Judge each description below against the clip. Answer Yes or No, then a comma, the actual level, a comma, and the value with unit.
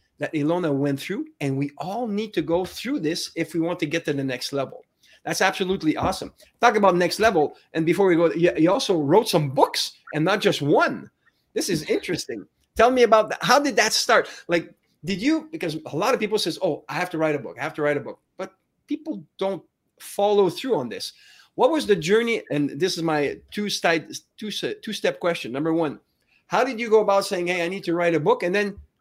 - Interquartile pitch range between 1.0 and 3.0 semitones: No, average, 4.8 semitones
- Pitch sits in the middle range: Yes, medium, 175 Hz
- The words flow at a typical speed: No, fast, 230 wpm